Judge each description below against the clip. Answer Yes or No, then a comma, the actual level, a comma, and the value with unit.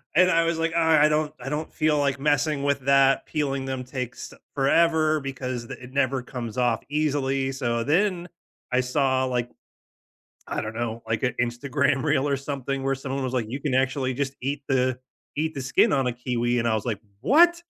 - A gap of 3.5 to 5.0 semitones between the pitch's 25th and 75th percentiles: No, average, 2.8 semitones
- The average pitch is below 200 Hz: Yes, low, 135 Hz